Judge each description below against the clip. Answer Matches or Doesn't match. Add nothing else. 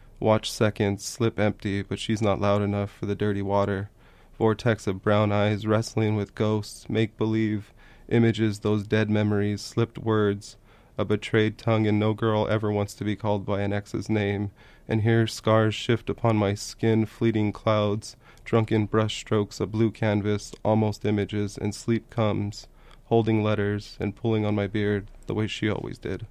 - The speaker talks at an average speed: Matches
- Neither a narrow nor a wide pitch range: Doesn't match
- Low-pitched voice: Matches